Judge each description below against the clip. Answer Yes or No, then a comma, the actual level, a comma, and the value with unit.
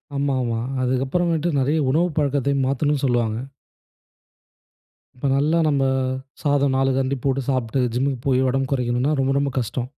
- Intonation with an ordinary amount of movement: No, narrow, 1.8 semitones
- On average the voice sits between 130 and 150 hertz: Yes, low, 135 Hz